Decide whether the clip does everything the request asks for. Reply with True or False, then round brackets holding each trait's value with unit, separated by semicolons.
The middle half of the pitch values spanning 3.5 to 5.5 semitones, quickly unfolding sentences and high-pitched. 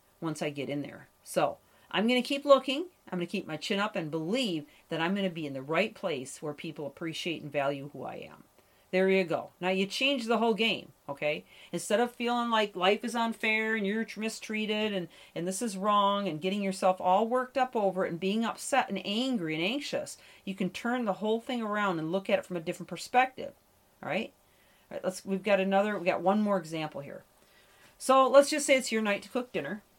True (4.6 semitones; 230 wpm; 195 Hz)